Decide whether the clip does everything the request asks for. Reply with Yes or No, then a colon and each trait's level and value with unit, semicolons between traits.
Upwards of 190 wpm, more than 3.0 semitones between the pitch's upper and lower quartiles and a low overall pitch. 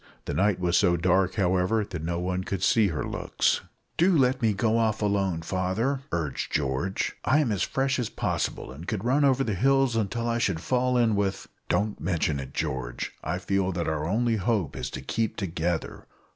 Yes: average, 200 wpm; average, 5.0 semitones; low, 100 Hz